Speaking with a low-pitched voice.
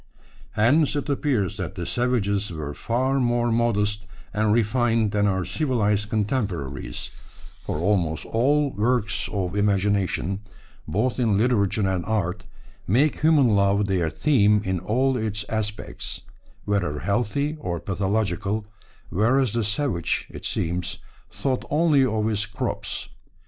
Yes: low, 105 Hz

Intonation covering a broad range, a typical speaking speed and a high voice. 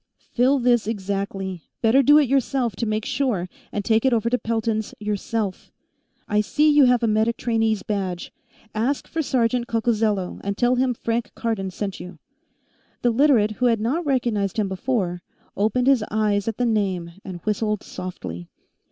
No: average, 3.4 semitones; average, 170 wpm; high, 220 Hz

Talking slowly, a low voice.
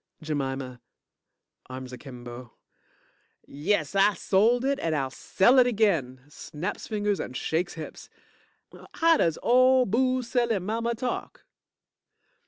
No: slow, 115 wpm; high, 195 Hz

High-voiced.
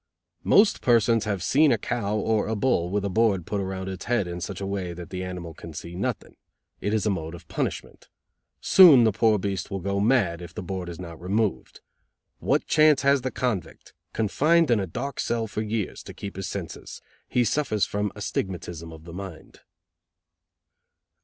No: low, 100 Hz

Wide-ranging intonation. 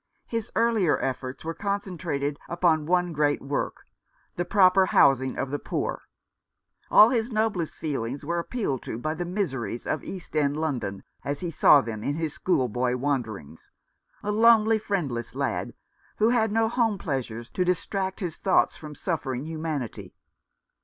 Yes: wide, 6.3 semitones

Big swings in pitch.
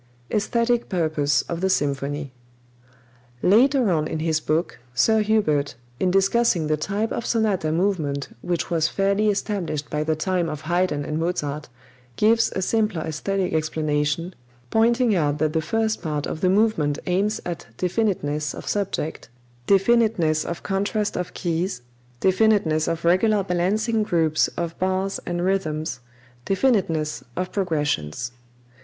No: average, 4.8 semitones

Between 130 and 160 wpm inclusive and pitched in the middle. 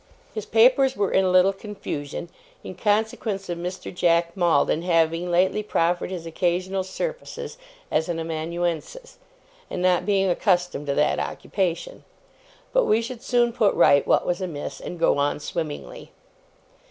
Yes: average, 150 wpm; medium, 180 Hz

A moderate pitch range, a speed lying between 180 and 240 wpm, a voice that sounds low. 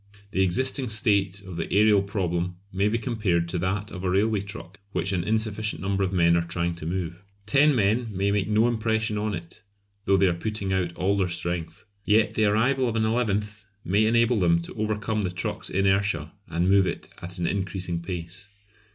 Yes: average, 3.3 semitones; average, 200 wpm; low, 100 Hz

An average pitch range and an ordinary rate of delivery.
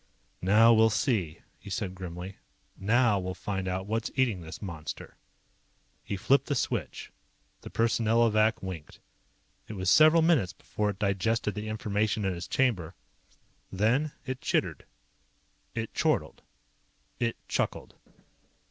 No: average, 3.6 semitones; slow, 130 wpm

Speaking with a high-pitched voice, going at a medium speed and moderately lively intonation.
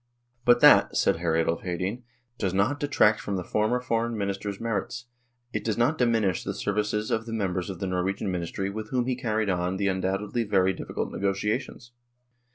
No: low, 105 Hz; average, 190 wpm; average, 3.6 semitones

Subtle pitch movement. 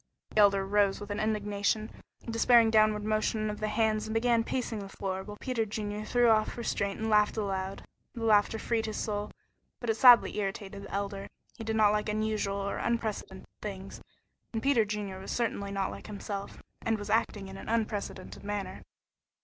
Yes: narrow, 1.7 semitones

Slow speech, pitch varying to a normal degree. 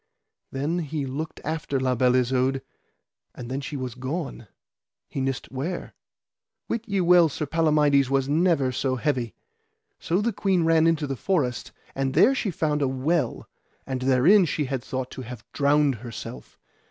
No: average, 165 wpm; average, 3.9 semitones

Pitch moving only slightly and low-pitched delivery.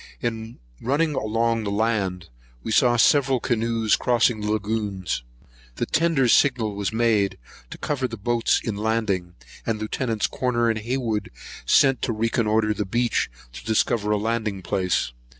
Yes: narrow, 2.1 semitones; low, 110 Hz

